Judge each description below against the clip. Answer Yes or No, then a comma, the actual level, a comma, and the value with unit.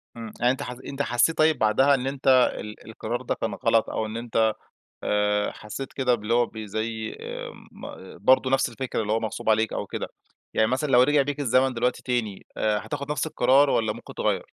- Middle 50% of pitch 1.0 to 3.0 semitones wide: No, average, 3.4 semitones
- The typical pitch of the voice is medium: No, low, 120 Hz